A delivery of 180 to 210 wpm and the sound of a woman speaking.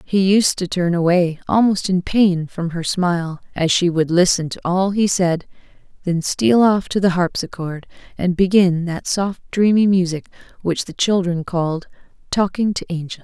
No: average, 170 wpm; female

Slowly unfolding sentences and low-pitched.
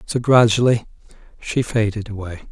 Yes: slow, 120 wpm; low, 110 Hz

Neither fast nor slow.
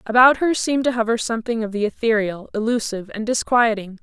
Yes: average, 180 wpm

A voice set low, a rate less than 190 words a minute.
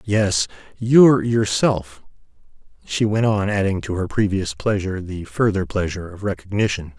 Yes: low, 100 Hz; slow, 135 wpm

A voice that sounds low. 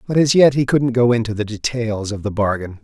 Yes: low, 115 Hz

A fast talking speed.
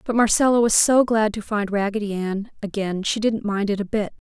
Yes: fast, 225 wpm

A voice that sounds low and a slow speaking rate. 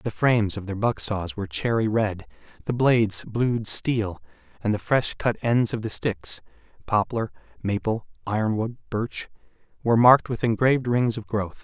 No: low, 110 Hz; average, 160 wpm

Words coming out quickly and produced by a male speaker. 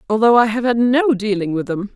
No: fast, 245 wpm; female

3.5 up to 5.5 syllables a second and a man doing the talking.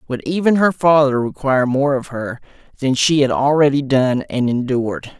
Yes: 5.0 syllables/s; male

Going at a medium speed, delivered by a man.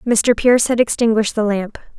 No: average, 180 wpm; female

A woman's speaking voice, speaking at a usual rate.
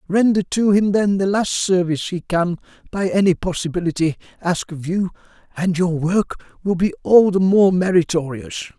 No: male; average, 165 wpm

